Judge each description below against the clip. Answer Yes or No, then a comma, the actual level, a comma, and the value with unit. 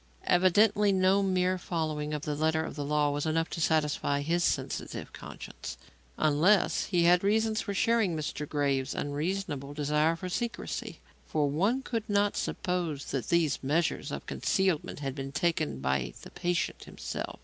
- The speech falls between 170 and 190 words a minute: No, average, 160 wpm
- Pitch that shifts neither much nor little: Yes, average, 4.3 semitones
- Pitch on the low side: No, medium, 160 Hz